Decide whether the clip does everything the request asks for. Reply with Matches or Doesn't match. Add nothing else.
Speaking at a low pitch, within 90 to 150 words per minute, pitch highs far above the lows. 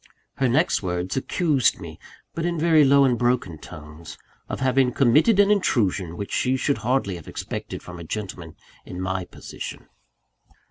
Doesn't match